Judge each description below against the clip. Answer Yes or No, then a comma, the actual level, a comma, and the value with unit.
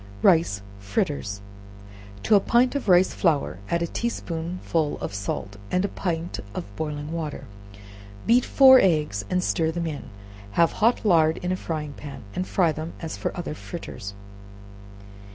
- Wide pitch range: No, average, 3.7 semitones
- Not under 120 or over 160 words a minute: Yes, average, 155 wpm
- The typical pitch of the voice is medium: Yes, medium, 165 Hz